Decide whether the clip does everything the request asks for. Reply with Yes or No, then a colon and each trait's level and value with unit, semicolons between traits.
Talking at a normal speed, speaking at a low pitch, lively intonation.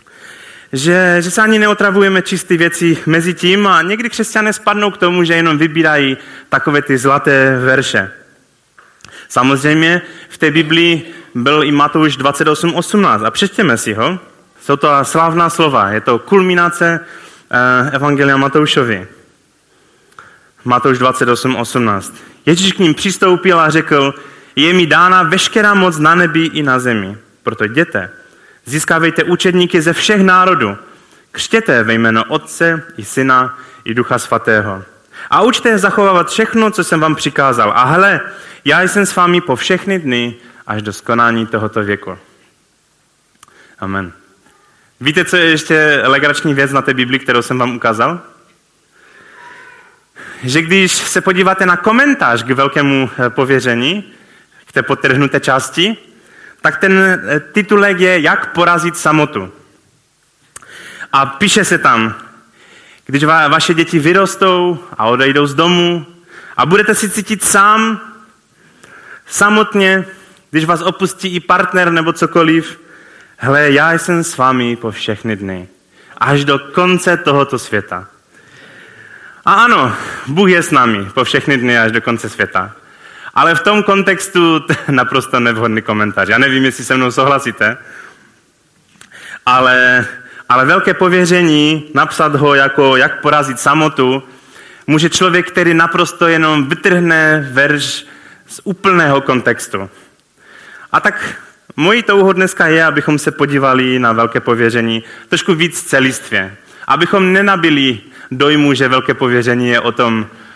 No: average, 130 wpm; medium, 155 Hz; wide, 5.8 semitones